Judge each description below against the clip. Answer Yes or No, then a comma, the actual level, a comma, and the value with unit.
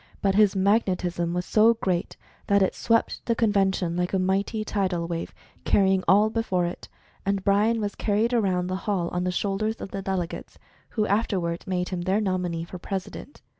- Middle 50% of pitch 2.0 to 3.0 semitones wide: Yes, narrow, 2.6 semitones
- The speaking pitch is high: Yes, high, 195 Hz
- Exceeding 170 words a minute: Yes, average, 180 wpm